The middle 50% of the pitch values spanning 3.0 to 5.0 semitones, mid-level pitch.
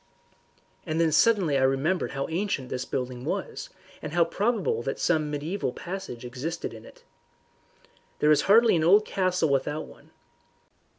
No: wide, 5.4 semitones; medium, 155 Hz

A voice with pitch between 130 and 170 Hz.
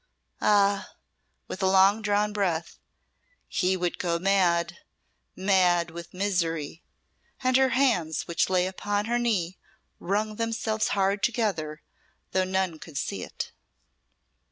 No: high, 190 Hz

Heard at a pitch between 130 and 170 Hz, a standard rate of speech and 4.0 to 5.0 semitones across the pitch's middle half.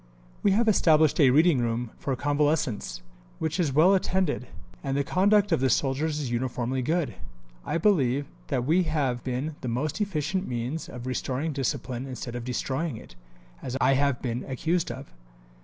Yes: medium, 140 Hz; average, 170 wpm; average, 4.3 semitones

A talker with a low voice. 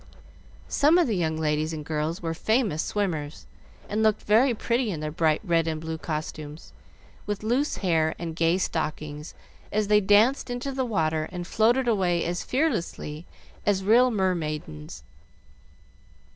No: medium, 175 Hz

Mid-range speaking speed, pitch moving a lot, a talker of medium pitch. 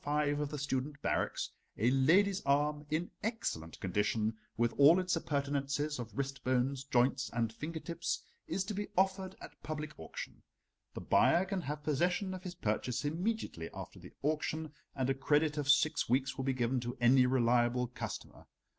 No: average, 175 wpm; average, 4.1 semitones; medium, 145 Hz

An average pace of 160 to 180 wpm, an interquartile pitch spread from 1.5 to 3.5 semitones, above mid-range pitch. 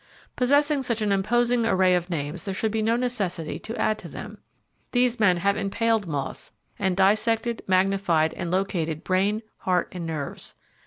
No: average, 165 wpm; average, 4.1 semitones; high, 195 Hz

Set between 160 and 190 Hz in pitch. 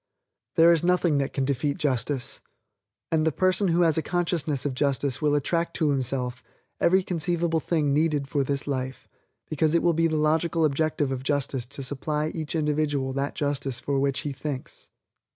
No: medium, 150 Hz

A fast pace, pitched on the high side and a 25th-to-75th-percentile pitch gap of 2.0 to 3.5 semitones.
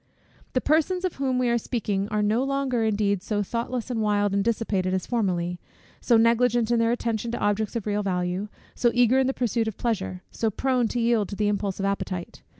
Yes: fast, 215 wpm; high, 225 Hz; average, 3.1 semitones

